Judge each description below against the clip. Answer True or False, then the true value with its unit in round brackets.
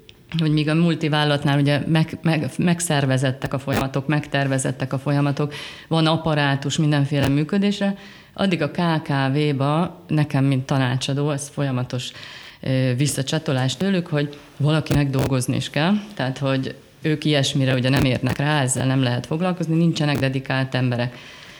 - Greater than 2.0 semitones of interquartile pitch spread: True (2.5 semitones)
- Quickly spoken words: False (130 wpm)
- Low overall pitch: False (145 Hz)